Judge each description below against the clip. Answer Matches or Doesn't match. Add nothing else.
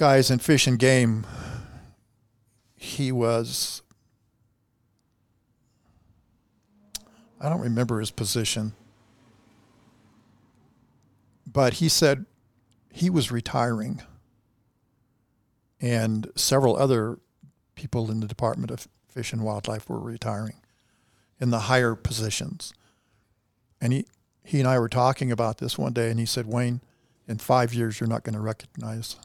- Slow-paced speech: Matches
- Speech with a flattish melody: Matches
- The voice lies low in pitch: Matches